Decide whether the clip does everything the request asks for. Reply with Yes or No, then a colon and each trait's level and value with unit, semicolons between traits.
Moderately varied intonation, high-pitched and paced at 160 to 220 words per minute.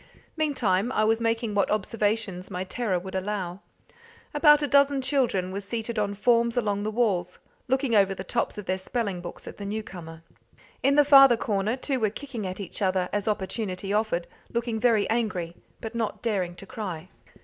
Yes: average, 3.8 semitones; high, 210 Hz; average, 180 wpm